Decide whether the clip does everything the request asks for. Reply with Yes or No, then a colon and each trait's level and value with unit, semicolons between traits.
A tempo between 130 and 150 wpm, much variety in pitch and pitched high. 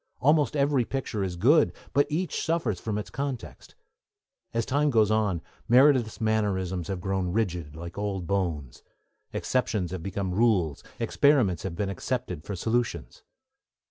No: average, 140 wpm; wide, 5.8 semitones; low, 105 Hz